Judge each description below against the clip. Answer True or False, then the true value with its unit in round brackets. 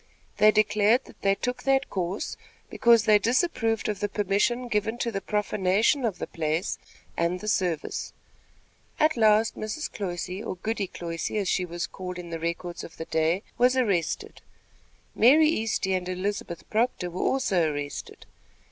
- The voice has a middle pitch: False (205 Hz)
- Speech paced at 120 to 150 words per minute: False (160 wpm)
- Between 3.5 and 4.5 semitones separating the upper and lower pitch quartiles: True (4.1 semitones)